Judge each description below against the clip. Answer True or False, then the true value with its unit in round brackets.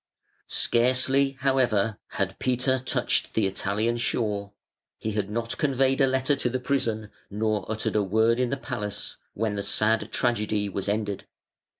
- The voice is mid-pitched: False (115 Hz)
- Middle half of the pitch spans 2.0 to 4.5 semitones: True (3.7 semitones)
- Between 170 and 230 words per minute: False (155 wpm)